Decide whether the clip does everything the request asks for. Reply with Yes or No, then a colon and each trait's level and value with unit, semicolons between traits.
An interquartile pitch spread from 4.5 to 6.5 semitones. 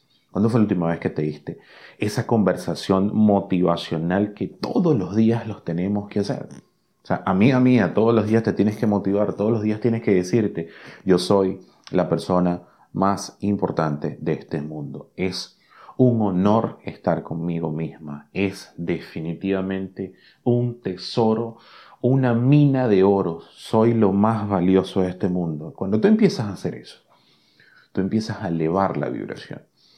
No: average, 4.0 semitones